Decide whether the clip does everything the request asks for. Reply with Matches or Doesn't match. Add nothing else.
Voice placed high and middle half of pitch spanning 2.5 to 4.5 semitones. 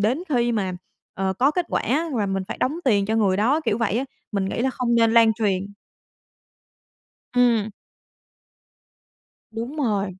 Matches